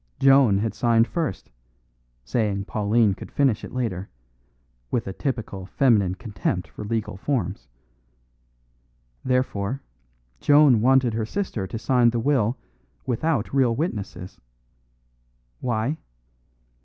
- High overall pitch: No, low, 115 Hz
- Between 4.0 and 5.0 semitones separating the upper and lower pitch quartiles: Yes, average, 4.4 semitones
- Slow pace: Yes, slow, 110 wpm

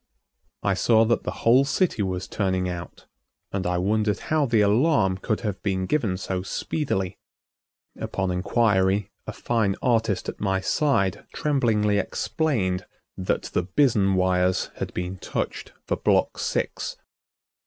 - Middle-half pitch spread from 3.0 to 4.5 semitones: Yes, average, 3.8 semitones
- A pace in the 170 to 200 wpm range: No, average, 140 wpm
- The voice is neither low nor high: No, low, 100 Hz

